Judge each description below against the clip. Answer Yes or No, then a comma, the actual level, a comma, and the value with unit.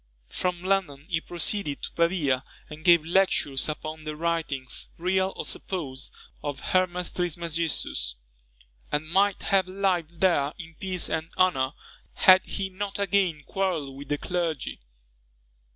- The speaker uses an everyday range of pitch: Yes, average, 3.6 semitones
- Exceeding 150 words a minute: No, slow, 135 wpm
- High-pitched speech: No, medium, 170 Hz